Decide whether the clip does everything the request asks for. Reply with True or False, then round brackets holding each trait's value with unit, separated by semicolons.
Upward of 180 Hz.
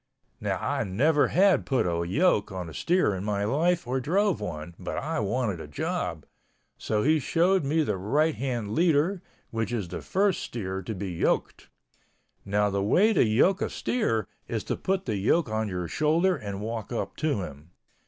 False (115 Hz)